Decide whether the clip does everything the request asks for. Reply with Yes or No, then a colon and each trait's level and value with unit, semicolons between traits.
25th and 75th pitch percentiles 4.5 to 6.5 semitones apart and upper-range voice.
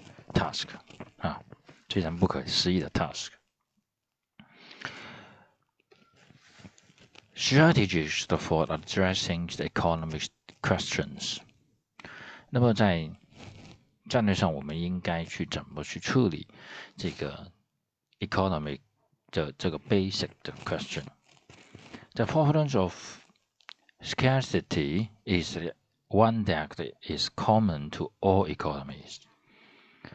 No: wide, 5.5 semitones; very low, 95 Hz